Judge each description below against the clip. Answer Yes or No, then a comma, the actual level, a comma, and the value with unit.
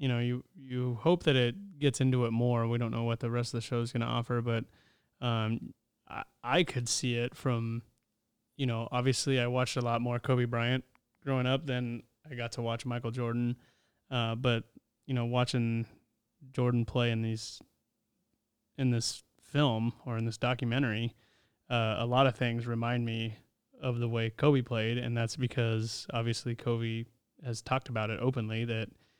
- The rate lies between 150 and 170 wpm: No, average, 185 wpm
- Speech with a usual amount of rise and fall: No, narrow, 1.6 semitones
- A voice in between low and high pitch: No, low, 120 Hz